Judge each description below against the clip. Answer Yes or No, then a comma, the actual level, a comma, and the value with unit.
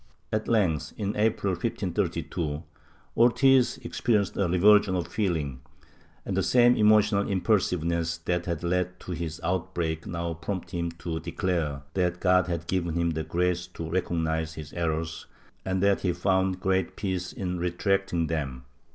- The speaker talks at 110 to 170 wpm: Yes, average, 150 wpm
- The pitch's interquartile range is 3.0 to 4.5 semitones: No, narrow, 2.6 semitones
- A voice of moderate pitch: No, very low, 90 Hz